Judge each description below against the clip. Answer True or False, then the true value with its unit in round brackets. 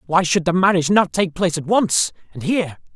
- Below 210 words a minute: False (225 wpm)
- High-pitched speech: False (175 Hz)